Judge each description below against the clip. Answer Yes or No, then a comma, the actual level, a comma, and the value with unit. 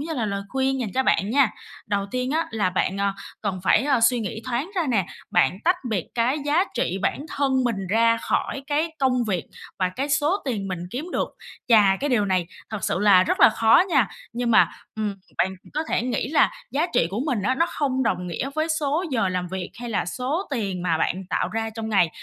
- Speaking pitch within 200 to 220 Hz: No, high, 230 Hz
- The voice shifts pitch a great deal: Yes, wide, 5.7 semitones